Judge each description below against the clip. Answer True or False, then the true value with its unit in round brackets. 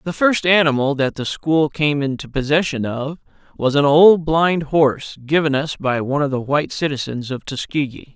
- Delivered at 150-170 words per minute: False (185 wpm)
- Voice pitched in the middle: True (145 Hz)